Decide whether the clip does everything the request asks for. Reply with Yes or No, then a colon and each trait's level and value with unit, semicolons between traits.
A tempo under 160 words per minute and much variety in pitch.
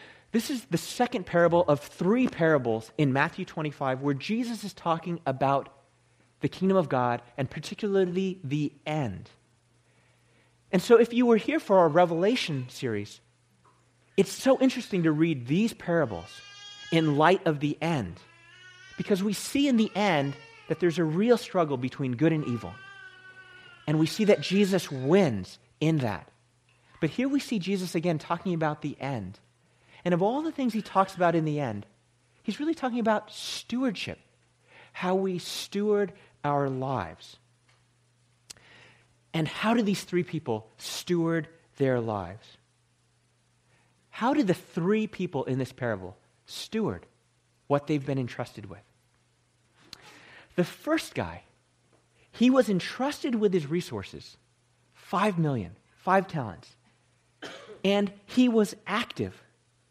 Yes: average, 140 wpm; wide, 8.5 semitones